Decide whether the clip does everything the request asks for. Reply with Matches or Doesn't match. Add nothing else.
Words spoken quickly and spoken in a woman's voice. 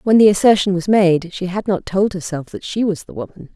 Matches